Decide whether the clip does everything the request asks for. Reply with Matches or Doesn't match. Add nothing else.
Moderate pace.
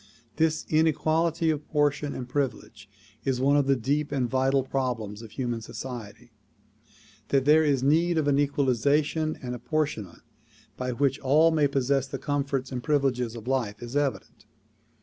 Matches